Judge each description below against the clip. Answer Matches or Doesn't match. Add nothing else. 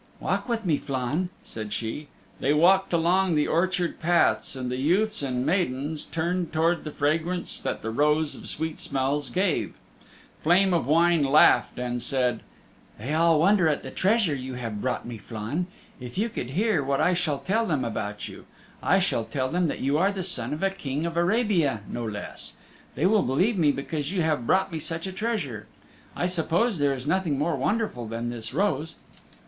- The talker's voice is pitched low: Doesn't match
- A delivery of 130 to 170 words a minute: Doesn't match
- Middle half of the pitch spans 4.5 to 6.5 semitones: Matches